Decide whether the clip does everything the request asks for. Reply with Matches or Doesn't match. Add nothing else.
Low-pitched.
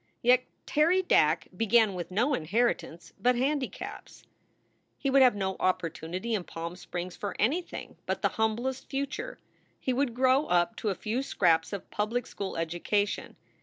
Doesn't match